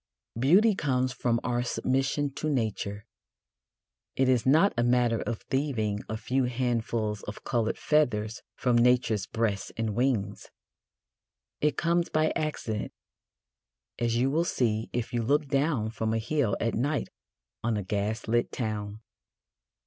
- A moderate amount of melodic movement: Yes, average, 3.6 semitones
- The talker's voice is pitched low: Yes, low, 120 Hz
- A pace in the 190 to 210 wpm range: No, average, 140 wpm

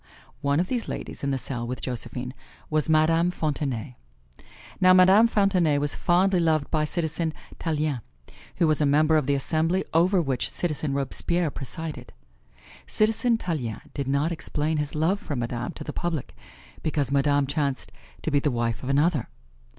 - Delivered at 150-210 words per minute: Yes, average, 165 wpm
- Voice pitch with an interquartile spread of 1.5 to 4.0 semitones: Yes, average, 3.4 semitones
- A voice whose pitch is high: No, medium, 155 Hz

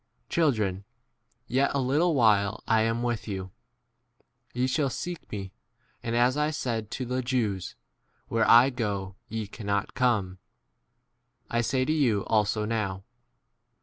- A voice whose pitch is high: No, low, 115 Hz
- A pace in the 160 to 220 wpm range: No, average, 140 wpm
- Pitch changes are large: No, average, 4.0 semitones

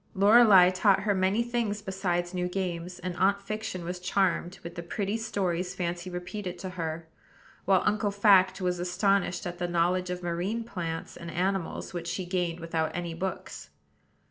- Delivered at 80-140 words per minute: No, average, 170 wpm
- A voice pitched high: No, medium, 180 Hz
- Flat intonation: Yes, narrow, 2.1 semitones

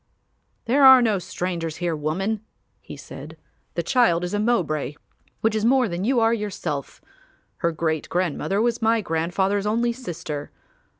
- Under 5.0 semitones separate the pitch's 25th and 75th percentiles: No, wide, 5.5 semitones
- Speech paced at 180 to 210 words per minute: No, average, 155 wpm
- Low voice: No, high, 195 Hz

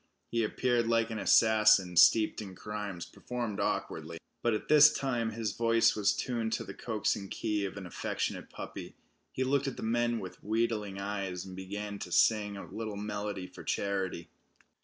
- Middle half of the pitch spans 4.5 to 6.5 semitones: No, average, 2.7 semitones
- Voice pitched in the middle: No, low, 105 Hz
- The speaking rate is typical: Yes, average, 175 wpm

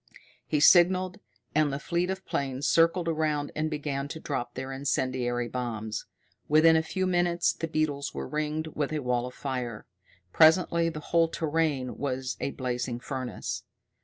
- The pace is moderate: Yes, average, 160 wpm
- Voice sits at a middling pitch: Yes, medium, 150 Hz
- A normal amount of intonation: Yes, average, 4.1 semitones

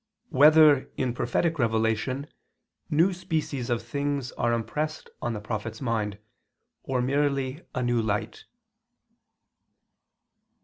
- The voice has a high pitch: No, low, 130 Hz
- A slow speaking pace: Yes, slow, 115 wpm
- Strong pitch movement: No, average, 4.1 semitones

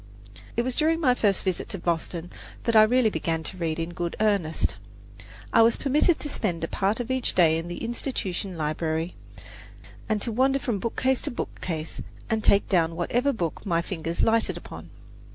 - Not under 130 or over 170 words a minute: No, average, 185 wpm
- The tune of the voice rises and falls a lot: Yes, wide, 6.1 semitones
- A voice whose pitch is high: Yes, high, 200 Hz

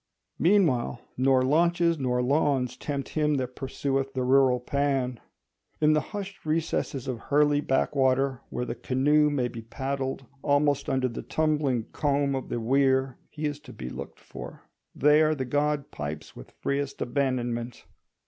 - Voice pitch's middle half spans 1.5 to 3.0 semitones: Yes, narrow, 2.5 semitones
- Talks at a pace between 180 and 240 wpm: No, average, 150 wpm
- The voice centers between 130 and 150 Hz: Yes, low, 135 Hz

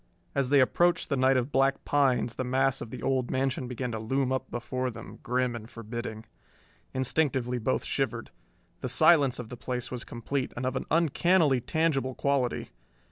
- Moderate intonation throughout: No, narrow, 1.9 semitones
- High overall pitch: No, low, 130 Hz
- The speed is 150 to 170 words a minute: No, average, 180 wpm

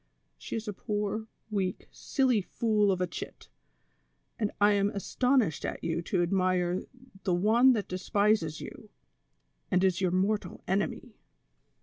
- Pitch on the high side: Yes, high, 200 Hz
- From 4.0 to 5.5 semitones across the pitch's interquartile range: No, average, 2.7 semitones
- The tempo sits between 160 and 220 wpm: No, average, 140 wpm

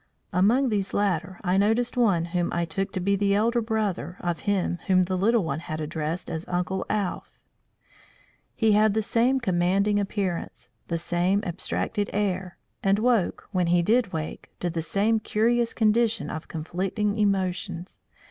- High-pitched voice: Yes, high, 195 Hz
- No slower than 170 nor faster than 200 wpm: No, average, 160 wpm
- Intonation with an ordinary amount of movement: Yes, average, 3.4 semitones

